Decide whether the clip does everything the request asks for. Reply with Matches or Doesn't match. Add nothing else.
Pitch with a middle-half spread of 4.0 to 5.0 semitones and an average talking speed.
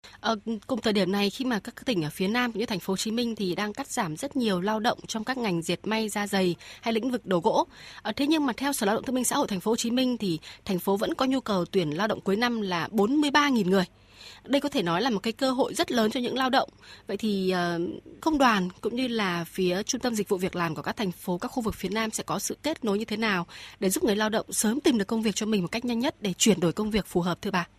Doesn't match